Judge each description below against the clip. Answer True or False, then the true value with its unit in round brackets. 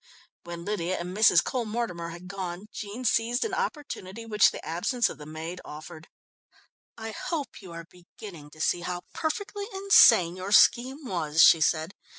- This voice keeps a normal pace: True (165 wpm)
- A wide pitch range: True (5.8 semitones)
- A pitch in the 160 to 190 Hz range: True (185 Hz)